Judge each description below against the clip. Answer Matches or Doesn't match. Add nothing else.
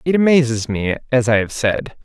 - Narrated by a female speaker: Doesn't match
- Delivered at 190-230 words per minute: Matches